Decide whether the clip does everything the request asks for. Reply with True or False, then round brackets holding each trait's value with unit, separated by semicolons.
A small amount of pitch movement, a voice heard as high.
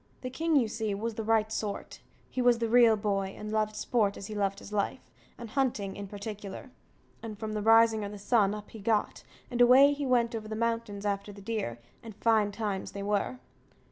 True (2.2 semitones; 215 Hz)